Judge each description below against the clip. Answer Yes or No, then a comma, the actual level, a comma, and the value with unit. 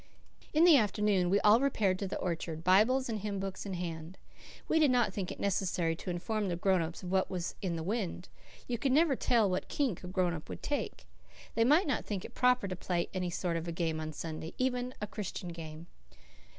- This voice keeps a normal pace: No, fast, 230 wpm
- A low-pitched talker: No, high, 190 Hz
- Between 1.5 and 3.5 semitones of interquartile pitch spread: No, average, 4.8 semitones